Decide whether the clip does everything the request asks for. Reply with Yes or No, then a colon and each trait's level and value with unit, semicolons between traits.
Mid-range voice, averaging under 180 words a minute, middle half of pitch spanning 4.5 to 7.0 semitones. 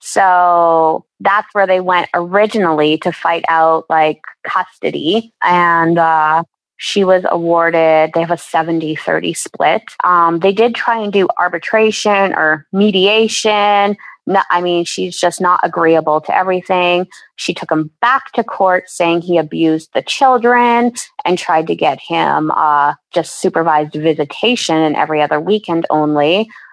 No: medium, 175 Hz; average, 145 wpm; average, 3.7 semitones